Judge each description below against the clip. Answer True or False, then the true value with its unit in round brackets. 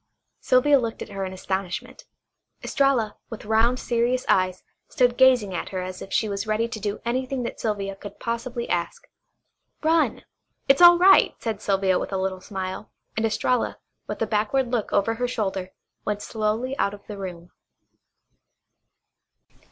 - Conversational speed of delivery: True (160 wpm)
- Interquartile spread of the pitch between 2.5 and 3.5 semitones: False (4.2 semitones)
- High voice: True (220 Hz)